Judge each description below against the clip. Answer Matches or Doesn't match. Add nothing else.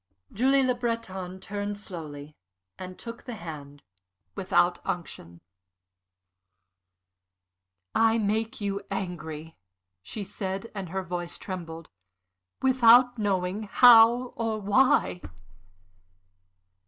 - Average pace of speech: Doesn't match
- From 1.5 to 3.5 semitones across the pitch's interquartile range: Doesn't match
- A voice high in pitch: Matches